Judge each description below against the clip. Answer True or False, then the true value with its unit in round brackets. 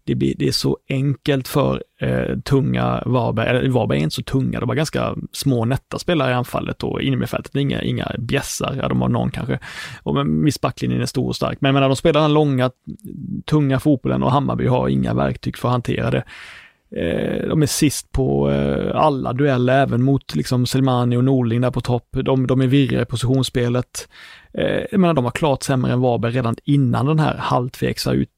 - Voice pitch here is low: True (125 Hz)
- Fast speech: True (205 wpm)